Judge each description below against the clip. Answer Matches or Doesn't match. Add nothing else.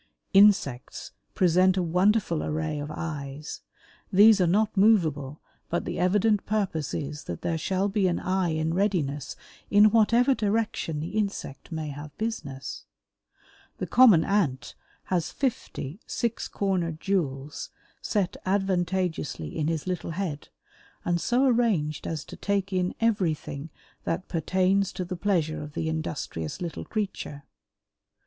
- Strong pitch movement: Doesn't match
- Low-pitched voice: Doesn't match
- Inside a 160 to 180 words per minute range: Doesn't match